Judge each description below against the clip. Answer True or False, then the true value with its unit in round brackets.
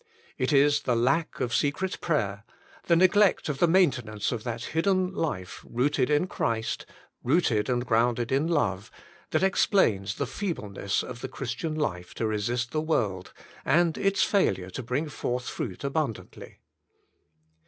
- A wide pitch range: True (6.3 semitones)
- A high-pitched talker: False (130 Hz)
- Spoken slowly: False (150 wpm)